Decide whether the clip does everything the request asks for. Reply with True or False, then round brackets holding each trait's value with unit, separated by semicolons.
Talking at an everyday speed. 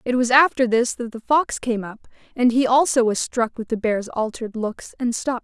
False (230 wpm)